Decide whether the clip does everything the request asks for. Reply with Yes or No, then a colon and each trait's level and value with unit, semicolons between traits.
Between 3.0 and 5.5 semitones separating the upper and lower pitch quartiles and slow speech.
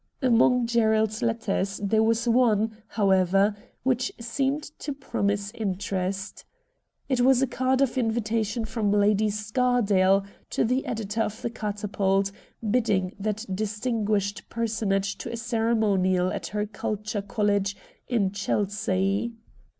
No: narrow, 2.6 semitones; slow, 125 wpm